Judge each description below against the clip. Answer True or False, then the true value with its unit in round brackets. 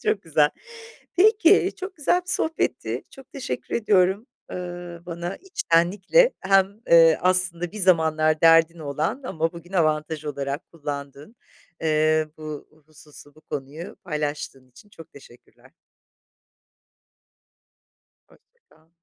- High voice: False (165 Hz)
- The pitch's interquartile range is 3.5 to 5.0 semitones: True (4.2 semitones)